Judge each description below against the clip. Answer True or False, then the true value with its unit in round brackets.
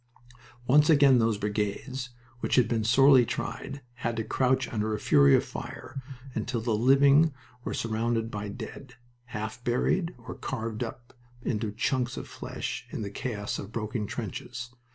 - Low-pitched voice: True (115 Hz)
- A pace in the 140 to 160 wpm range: True (155 wpm)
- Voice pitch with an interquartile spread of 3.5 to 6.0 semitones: False (3.1 semitones)